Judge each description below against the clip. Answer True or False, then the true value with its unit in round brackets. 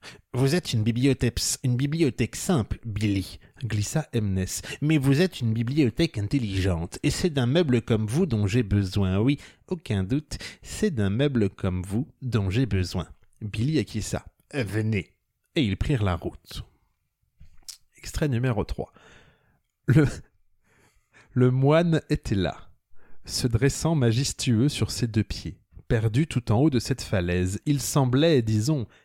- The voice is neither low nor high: False (115 Hz)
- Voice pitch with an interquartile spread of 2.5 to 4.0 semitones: False (5.5 semitones)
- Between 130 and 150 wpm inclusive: True (145 wpm)